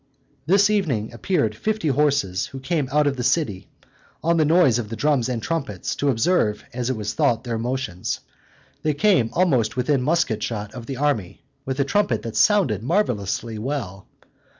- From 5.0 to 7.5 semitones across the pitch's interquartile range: Yes, wide, 5.4 semitones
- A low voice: Yes, low, 130 Hz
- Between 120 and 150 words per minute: No, average, 175 wpm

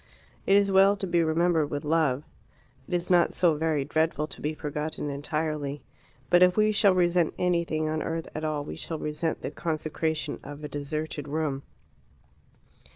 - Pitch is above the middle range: No, medium, 155 Hz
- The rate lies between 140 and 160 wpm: No, average, 170 wpm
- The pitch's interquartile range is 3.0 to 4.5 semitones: No, narrow, 2.6 semitones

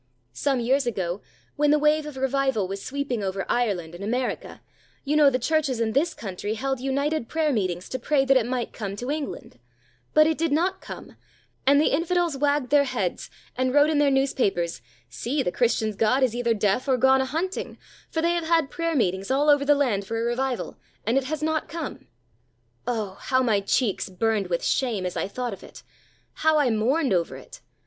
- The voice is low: No, very high, 260 Hz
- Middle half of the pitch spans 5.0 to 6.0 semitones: Yes, average, 5.3 semitones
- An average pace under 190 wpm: No, fast, 205 wpm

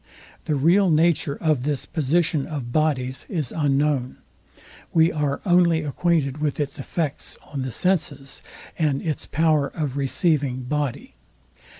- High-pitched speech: No, medium, 150 Hz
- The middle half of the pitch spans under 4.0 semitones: Yes, average, 2.8 semitones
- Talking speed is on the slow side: Yes, slow, 130 wpm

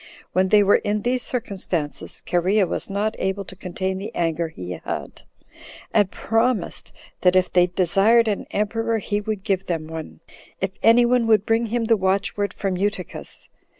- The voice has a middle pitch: No, high, 200 Hz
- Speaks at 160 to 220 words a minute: Yes, average, 170 wpm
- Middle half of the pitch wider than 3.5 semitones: No, average, 3.2 semitones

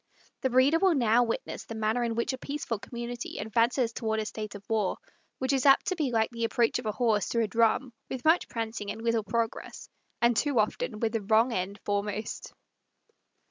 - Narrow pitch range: Yes, narrow, 2.2 semitones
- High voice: Yes, high, 230 Hz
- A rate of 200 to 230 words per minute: Yes, fast, 205 wpm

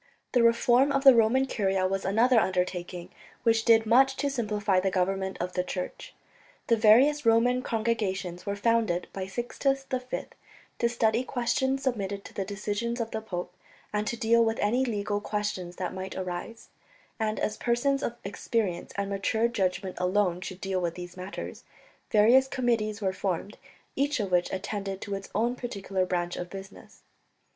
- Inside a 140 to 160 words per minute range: No, average, 170 wpm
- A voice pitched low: No, high, 210 Hz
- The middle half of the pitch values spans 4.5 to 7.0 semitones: No, average, 3.8 semitones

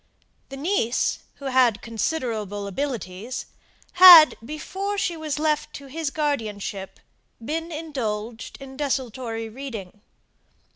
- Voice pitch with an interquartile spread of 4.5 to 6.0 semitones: Yes, wide, 5.5 semitones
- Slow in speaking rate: Yes, slow, 105 wpm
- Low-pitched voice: No, very high, 265 Hz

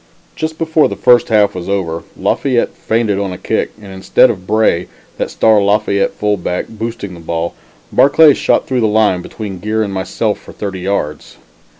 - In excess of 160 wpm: Yes, average, 180 wpm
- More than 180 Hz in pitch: No, low, 105 Hz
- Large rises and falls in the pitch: No, average, 3.0 semitones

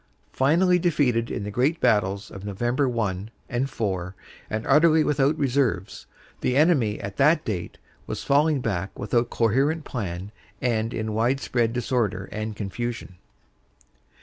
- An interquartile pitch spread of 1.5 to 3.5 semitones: No, average, 5.0 semitones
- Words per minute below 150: Yes, average, 140 wpm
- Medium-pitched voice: No, low, 120 Hz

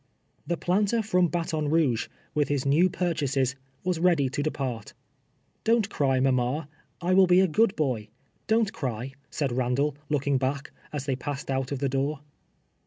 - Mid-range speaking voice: Yes, medium, 145 Hz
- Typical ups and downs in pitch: Yes, average, 4.7 semitones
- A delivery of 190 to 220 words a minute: No, average, 175 wpm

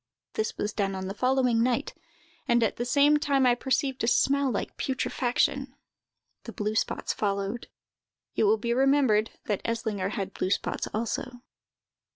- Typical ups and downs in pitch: Yes, average, 4.0 semitones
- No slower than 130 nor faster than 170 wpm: Yes, average, 160 wpm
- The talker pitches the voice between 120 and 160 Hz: No, high, 235 Hz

